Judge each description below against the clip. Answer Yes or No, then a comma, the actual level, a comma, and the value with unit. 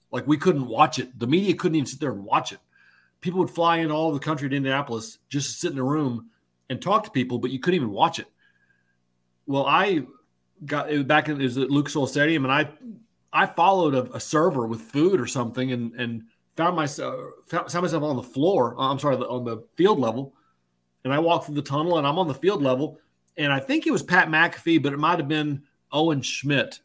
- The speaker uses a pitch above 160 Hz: No, medium, 140 Hz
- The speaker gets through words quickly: Yes, fast, 225 wpm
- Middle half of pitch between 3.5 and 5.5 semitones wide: Yes, average, 4.3 semitones